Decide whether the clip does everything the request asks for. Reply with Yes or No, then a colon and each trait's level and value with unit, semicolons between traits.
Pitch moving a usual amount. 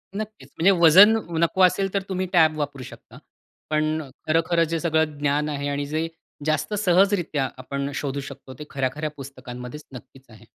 Yes: average, 3.6 semitones